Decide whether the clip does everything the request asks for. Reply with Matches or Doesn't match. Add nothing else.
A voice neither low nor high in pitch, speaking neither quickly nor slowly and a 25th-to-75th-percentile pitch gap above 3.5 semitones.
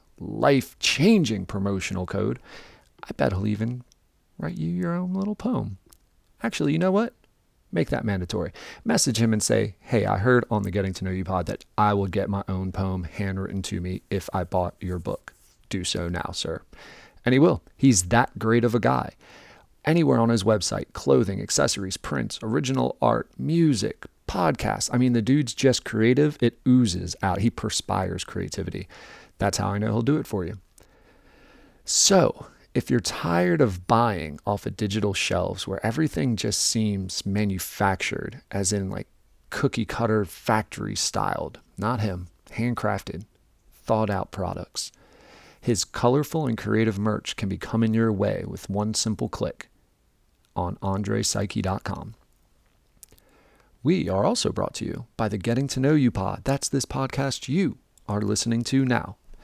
Doesn't match